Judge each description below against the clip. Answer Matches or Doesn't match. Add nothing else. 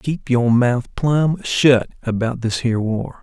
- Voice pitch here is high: Doesn't match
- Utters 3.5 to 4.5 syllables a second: Matches